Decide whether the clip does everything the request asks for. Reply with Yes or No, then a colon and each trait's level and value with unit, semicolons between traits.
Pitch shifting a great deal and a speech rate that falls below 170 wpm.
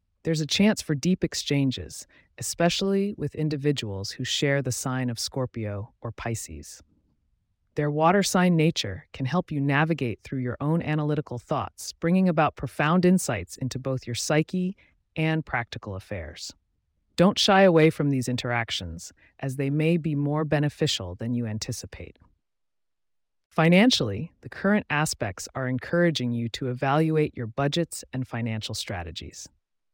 Yes: wide, 7.2 semitones; average, 140 wpm